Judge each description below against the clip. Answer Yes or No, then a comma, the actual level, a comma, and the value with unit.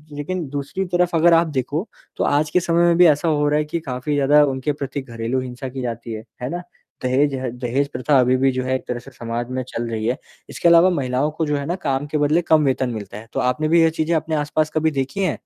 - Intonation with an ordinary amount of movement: Yes, average, 3.8 semitones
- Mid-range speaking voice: Yes, medium, 145 Hz